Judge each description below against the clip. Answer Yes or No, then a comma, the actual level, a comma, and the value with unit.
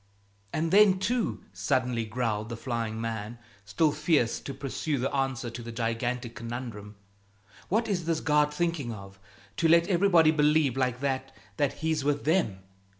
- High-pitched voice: No, low, 135 Hz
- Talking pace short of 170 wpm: Yes, average, 155 wpm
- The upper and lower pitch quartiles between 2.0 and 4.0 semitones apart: No, wide, 5.4 semitones